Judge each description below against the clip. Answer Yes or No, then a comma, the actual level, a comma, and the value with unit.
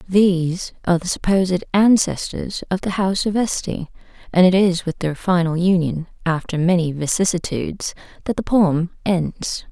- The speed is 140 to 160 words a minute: Yes, average, 150 wpm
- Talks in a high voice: No, medium, 180 Hz